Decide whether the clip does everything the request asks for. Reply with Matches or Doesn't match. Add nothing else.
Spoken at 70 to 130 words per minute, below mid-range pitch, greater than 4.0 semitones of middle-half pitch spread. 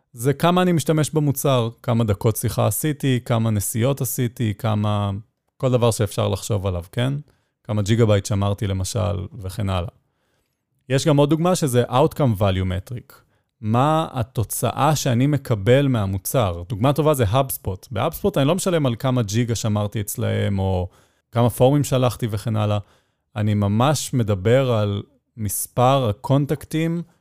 Doesn't match